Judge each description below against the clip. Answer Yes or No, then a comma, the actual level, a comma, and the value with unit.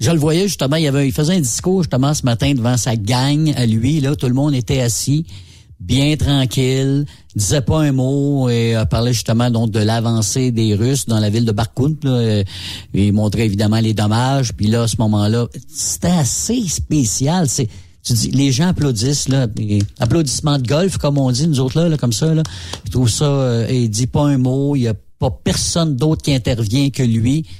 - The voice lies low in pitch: Yes, low, 130 Hz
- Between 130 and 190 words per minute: No, average, 205 wpm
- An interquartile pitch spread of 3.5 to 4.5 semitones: Yes, average, 4.1 semitones